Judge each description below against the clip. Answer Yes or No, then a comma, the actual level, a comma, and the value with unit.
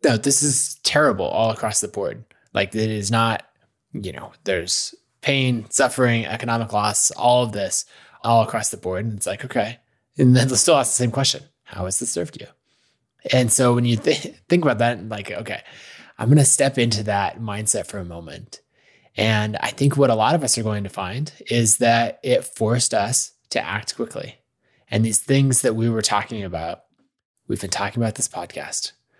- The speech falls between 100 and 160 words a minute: No, average, 200 wpm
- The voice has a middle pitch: No, low, 115 Hz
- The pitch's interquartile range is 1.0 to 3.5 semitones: Yes, average, 3.1 semitones